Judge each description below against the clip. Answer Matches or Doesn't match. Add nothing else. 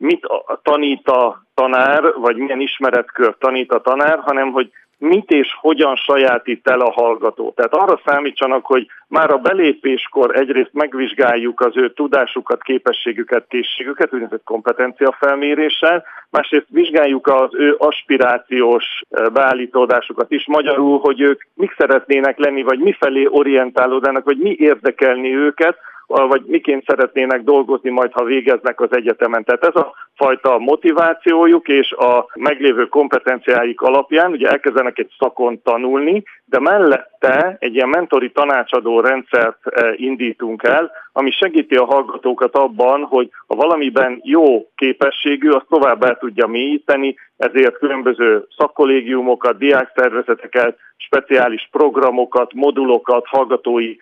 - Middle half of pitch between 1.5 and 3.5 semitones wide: Matches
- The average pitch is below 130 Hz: Doesn't match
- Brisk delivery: Doesn't match